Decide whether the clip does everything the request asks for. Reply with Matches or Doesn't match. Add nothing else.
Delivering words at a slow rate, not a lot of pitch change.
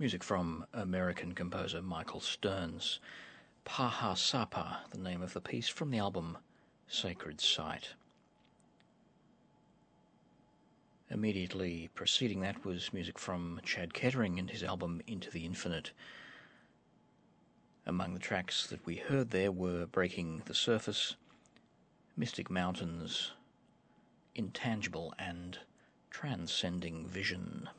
Matches